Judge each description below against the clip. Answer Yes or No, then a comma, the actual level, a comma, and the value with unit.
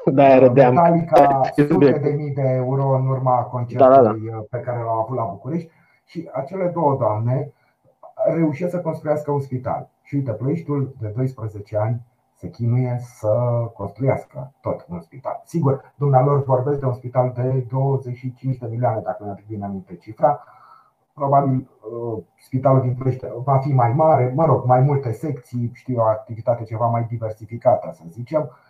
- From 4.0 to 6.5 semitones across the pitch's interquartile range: No, average, 3.2 semitones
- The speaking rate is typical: Yes, average, 155 wpm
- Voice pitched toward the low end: Yes, low, 130 Hz